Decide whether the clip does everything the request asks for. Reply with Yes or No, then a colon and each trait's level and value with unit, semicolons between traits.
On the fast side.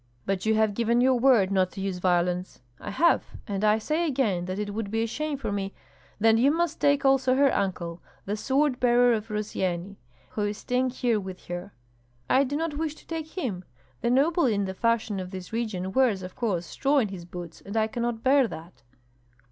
Yes: fast, 215 wpm